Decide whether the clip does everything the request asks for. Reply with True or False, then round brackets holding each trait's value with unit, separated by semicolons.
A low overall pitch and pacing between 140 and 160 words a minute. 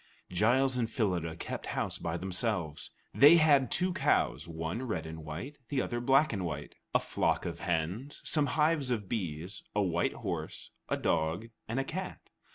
False (105 Hz; 170 wpm)